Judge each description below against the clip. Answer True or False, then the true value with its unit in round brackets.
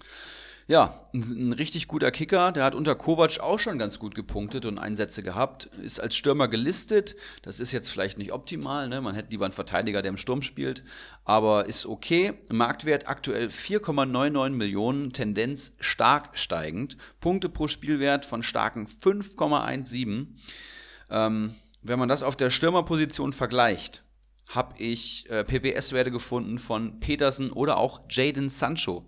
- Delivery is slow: False (150 wpm)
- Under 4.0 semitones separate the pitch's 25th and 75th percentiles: False (4.7 semitones)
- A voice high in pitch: False (125 Hz)